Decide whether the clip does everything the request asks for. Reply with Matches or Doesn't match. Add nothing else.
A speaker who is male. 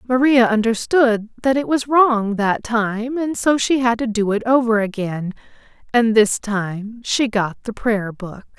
Doesn't match